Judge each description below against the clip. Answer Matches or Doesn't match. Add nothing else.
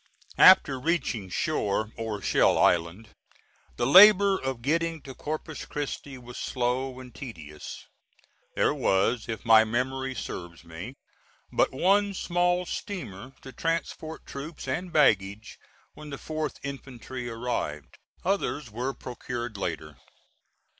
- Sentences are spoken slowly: Matches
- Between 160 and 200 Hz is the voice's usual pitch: Doesn't match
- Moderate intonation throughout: Doesn't match